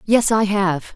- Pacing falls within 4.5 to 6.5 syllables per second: No, 3.3 syllables/s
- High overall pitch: Yes, high, 200 Hz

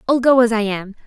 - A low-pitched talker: No, high, 230 Hz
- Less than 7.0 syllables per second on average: Yes, 6.2 syllables/s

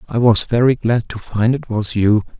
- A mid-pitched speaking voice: No, low, 115 Hz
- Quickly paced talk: Yes, fast, 225 wpm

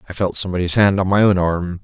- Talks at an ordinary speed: No, fast, 260 wpm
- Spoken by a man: Yes, male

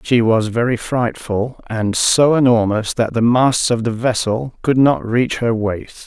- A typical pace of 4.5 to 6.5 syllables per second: No, 4.0 syllables/s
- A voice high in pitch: No, low, 115 Hz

